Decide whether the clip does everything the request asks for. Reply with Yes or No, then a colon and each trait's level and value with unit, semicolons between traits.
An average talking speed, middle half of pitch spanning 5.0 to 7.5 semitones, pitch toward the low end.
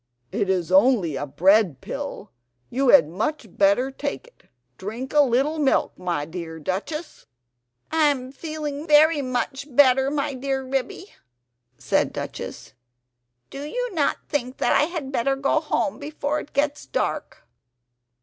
No: average, 145 wpm; wide, 5.4 semitones; very high, 270 Hz